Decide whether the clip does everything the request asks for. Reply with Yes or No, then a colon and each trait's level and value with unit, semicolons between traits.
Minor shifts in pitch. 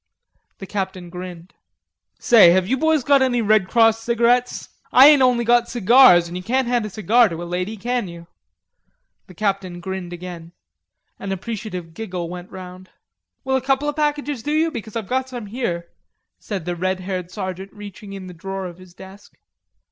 No: average, 4.9 semitones